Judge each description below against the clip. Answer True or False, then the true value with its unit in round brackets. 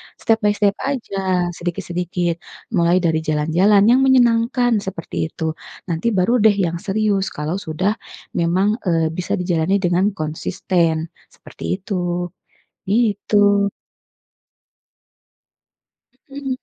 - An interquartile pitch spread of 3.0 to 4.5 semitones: True (3.6 semitones)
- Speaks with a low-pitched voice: False (190 Hz)